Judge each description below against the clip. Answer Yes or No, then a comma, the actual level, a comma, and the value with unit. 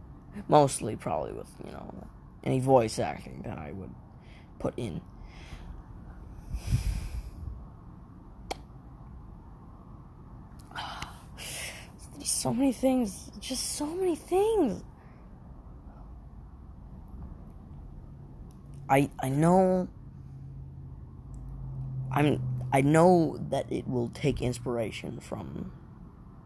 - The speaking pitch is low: Yes, low, 130 Hz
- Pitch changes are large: Yes, wide, 8.2 semitones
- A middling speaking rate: No, slow, 75 wpm